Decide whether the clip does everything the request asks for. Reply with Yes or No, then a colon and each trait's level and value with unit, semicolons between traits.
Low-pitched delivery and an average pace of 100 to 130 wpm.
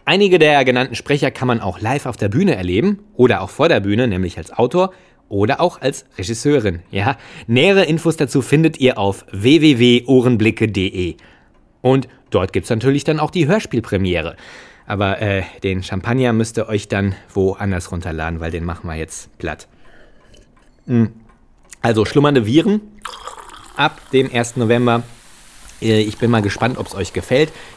No: low, 115 Hz; average, 155 wpm